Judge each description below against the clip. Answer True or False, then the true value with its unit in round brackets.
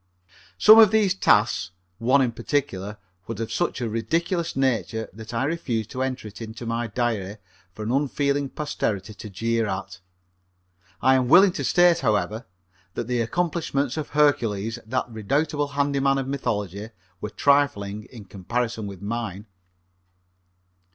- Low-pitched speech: True (120 Hz)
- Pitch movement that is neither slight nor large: True (4.8 semitones)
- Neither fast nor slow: True (150 wpm)